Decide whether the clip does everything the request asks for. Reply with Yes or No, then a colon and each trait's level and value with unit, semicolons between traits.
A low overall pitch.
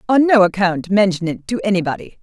No: high, 195 Hz